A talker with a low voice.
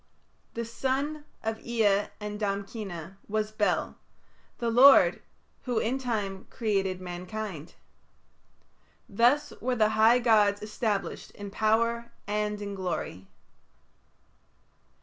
No: high, 215 Hz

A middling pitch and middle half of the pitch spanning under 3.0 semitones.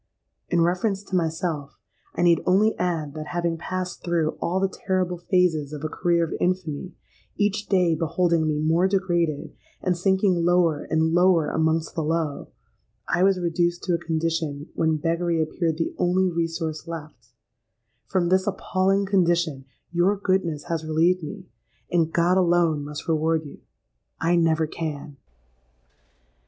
Yes: medium, 170 Hz; narrow, 2.4 semitones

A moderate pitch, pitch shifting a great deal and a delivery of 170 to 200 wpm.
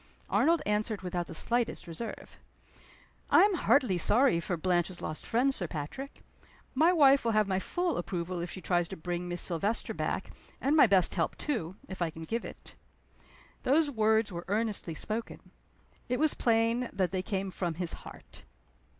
No: high, 200 Hz; wide, 5.7 semitones; average, 175 wpm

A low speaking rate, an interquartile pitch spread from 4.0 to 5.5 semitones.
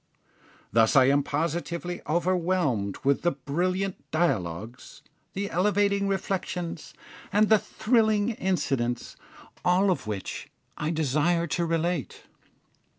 Yes: slow, 105 wpm; average, 5.2 semitones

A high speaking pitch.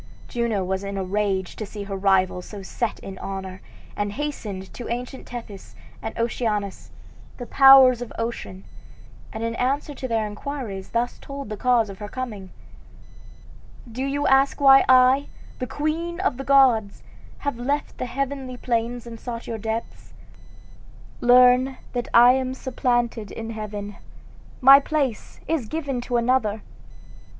Yes: high, 240 Hz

